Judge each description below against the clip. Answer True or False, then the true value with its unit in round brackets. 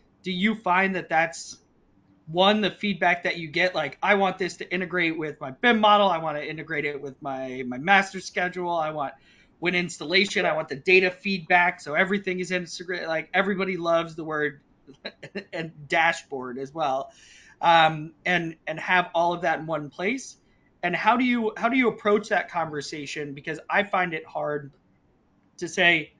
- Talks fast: False (185 wpm)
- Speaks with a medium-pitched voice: True (170 Hz)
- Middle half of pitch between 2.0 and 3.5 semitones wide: True (3.2 semitones)